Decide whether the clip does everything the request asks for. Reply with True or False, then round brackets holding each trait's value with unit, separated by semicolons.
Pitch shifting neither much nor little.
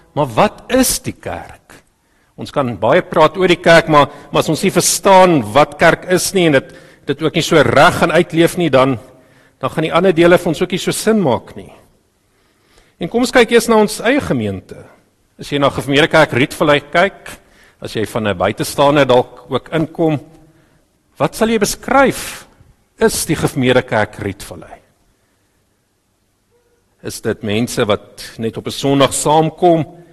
False (6.1 semitones)